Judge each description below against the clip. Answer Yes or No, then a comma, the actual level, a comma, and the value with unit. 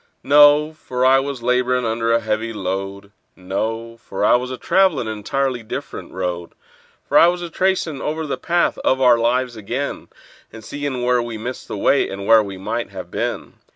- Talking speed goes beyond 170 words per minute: Yes, average, 180 wpm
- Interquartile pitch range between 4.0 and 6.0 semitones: Yes, average, 4.3 semitones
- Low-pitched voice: Yes, low, 120 Hz